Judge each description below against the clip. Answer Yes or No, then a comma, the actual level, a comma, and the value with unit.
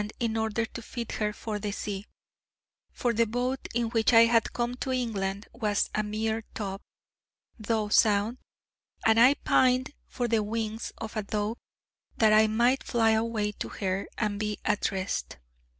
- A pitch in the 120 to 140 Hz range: No, high, 220 Hz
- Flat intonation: Yes, narrow, 2.0 semitones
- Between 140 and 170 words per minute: Yes, average, 165 wpm